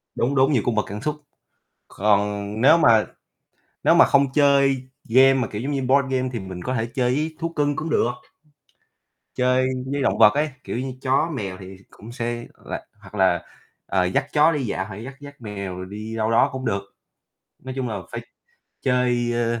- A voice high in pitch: No, low, 125 Hz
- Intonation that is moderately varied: Yes, average, 4.3 semitones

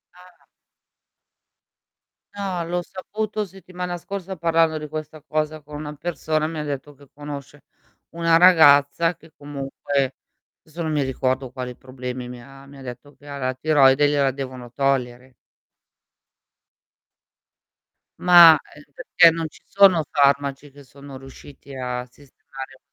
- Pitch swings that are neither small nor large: Yes, average, 3.4 semitones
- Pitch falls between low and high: Yes, medium, 145 Hz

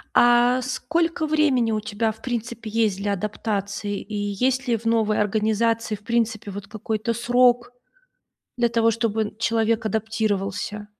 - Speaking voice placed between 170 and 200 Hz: No, high, 225 Hz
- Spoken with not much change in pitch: Yes, narrow, 2.3 semitones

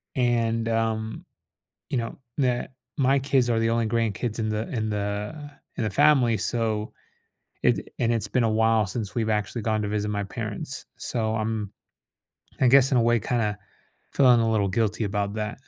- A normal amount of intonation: No, narrow, 2.0 semitones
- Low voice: Yes, low, 115 Hz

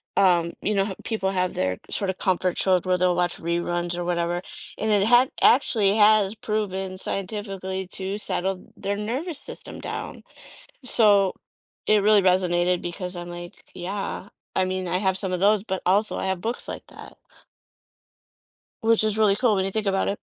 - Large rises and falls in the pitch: No, narrow, 2.5 semitones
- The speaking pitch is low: No, high, 190 Hz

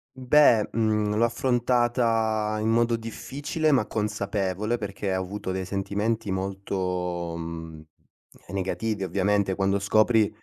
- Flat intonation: No, average, 3.0 semitones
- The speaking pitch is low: Yes, low, 105 Hz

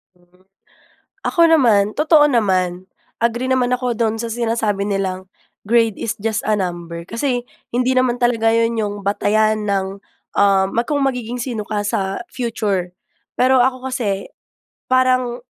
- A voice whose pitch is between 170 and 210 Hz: No, high, 225 Hz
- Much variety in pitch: No, average, 3.9 semitones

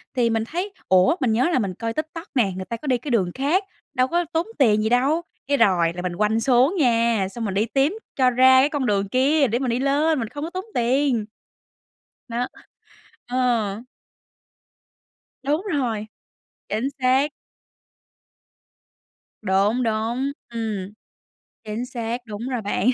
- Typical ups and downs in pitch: Yes, average, 4.2 semitones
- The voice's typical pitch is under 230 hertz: No, high, 245 Hz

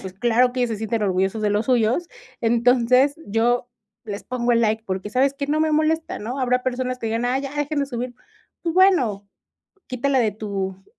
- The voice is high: Yes, high, 245 Hz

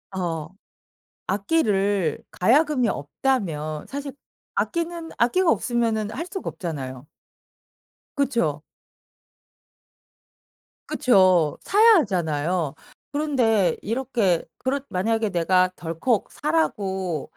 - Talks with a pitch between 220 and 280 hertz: No, high, 205 Hz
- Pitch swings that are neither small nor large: No, wide, 7.8 semitones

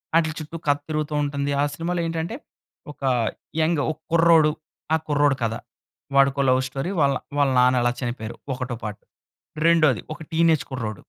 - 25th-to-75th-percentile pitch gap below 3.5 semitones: No, average, 3.9 semitones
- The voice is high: No, medium, 145 Hz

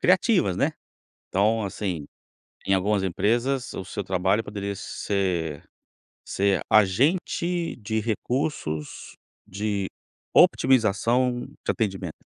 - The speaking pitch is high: No, low, 105 Hz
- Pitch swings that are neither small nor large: Yes, average, 4.3 semitones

